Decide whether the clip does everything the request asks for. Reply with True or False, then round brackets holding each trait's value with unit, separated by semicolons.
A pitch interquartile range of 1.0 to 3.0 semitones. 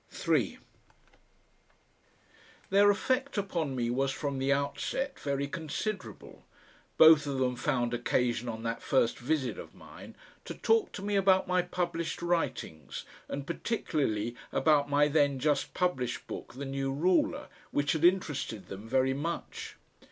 False (5.2 semitones)